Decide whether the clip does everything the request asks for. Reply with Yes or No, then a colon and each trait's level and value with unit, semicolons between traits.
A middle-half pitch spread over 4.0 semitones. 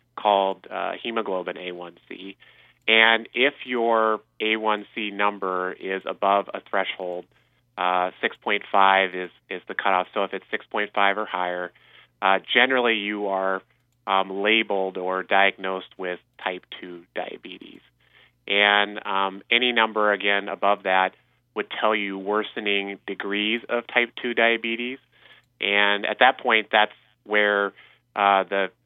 No: narrow, 2.5 semitones